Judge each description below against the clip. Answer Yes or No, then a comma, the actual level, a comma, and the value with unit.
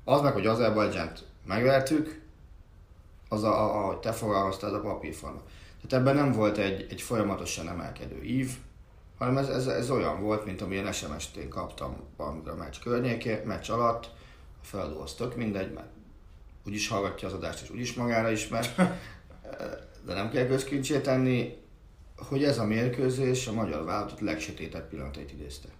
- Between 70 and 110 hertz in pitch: Yes, low, 105 Hz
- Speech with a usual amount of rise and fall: No, wide, 6.3 semitones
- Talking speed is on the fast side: Yes, fast, 160 wpm